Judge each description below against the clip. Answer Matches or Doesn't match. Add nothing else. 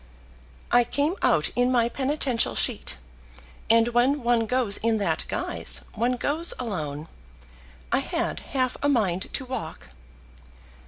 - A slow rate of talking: Matches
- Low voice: Doesn't match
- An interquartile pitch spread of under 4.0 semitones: Matches